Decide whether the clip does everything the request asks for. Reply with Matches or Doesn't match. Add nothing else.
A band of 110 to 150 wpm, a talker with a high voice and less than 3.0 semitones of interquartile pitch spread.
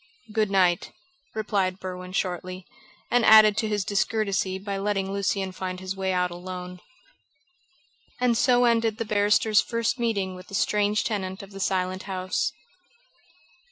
Matches